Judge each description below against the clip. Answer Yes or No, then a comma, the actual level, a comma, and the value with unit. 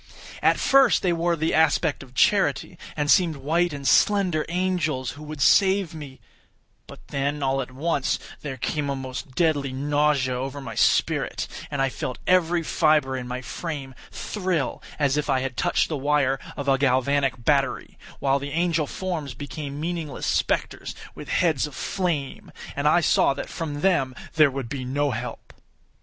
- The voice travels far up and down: No, average, 3.5 semitones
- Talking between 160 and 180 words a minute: Yes, average, 170 wpm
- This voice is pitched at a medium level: Yes, medium, 145 Hz